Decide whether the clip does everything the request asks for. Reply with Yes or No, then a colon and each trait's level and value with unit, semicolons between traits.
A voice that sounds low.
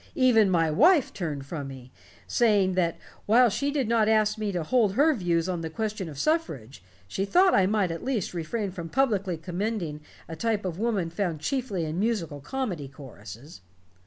No: high, 190 Hz